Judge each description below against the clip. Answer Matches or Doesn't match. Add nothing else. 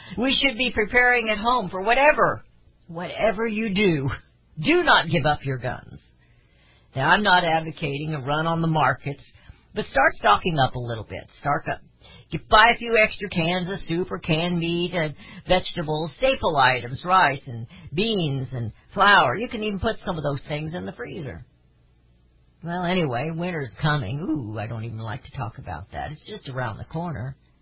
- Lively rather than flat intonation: Matches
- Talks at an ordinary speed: Matches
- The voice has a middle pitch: Matches